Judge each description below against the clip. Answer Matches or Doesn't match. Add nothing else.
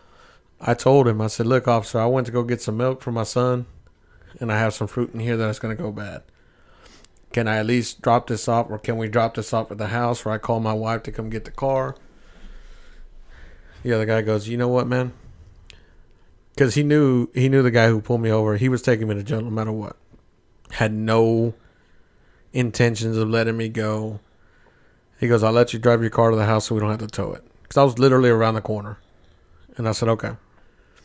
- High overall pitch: Doesn't match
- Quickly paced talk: Matches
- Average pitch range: Doesn't match